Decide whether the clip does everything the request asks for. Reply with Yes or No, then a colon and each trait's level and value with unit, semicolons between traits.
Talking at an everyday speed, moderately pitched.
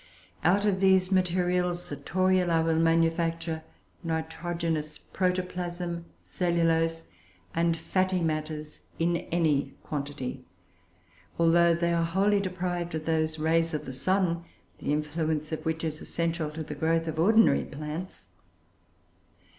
No: slow, 125 wpm; medium, 165 Hz